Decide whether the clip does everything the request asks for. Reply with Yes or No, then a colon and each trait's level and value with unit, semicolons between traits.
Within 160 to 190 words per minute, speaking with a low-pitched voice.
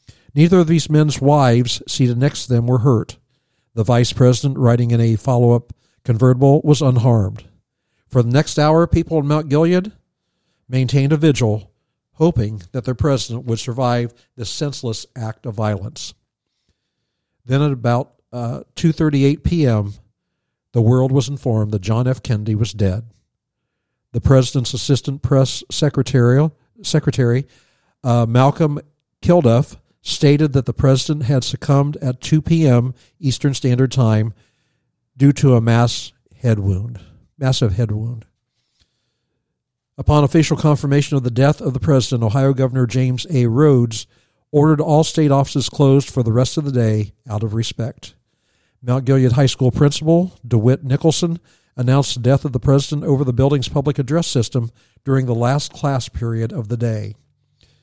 No: average, 150 wpm; low, 130 Hz